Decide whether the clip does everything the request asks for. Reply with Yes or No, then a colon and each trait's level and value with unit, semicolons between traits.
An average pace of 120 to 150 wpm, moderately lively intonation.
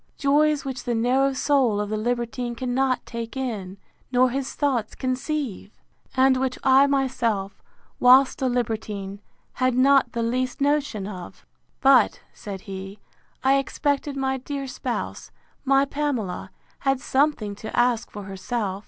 Yes: average, 140 wpm; average, 3.6 semitones